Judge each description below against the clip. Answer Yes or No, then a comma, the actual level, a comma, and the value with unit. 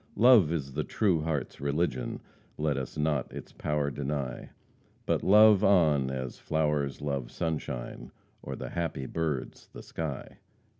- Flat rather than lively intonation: No, average, 3.3 semitones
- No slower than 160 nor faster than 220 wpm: No, average, 140 wpm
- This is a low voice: Yes, very low, 75 Hz